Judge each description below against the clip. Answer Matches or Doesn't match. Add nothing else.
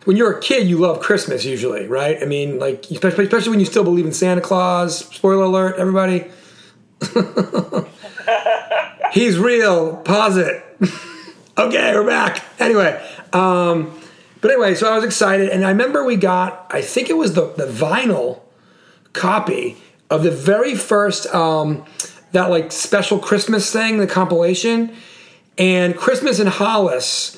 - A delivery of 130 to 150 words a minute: Matches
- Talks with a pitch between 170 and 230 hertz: Matches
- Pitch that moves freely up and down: Doesn't match